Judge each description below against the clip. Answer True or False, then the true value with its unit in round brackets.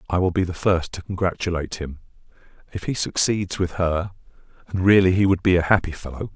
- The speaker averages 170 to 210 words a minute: True (200 wpm)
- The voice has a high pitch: False (90 Hz)